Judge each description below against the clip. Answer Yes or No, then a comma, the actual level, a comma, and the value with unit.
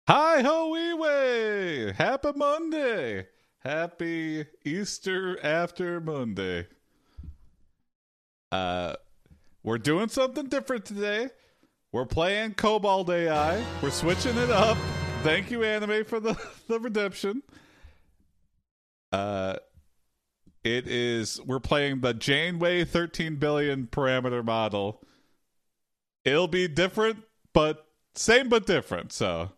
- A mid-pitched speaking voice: Yes, medium, 165 Hz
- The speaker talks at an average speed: No, slow, 105 wpm